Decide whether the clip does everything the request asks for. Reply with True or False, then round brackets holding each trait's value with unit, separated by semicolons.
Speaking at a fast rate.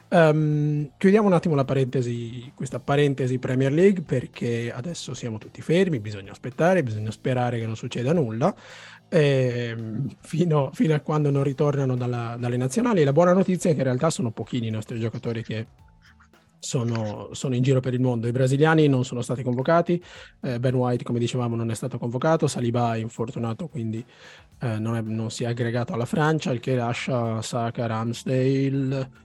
True (175 wpm)